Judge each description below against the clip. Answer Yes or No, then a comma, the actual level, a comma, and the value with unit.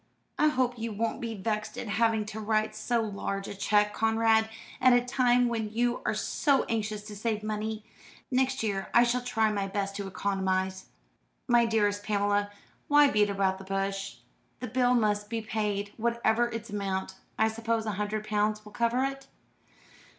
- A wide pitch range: No, narrow, 2.5 semitones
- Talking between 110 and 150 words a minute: No, average, 175 wpm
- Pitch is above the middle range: Yes, high, 215 Hz